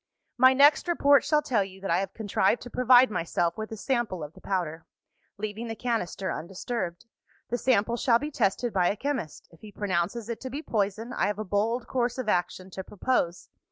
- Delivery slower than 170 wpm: No, fast, 205 wpm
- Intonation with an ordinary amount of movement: Yes, average, 4.6 semitones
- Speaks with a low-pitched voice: No, high, 215 Hz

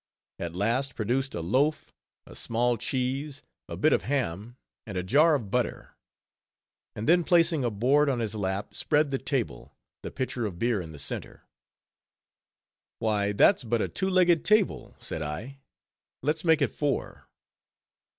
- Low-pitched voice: Yes, low, 125 Hz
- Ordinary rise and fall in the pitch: No, wide, 6.0 semitones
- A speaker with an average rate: Yes, average, 160 wpm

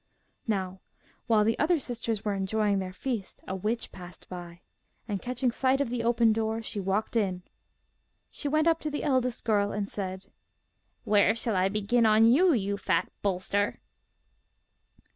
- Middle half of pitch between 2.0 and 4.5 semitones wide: Yes, average, 3.7 semitones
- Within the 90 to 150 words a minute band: No, average, 160 wpm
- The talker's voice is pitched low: No, high, 215 Hz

